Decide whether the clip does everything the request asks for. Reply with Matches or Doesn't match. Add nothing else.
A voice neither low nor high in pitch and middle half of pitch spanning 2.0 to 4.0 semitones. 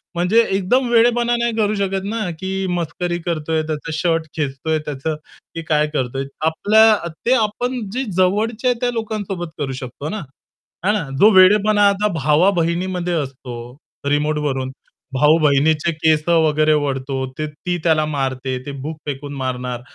Doesn't match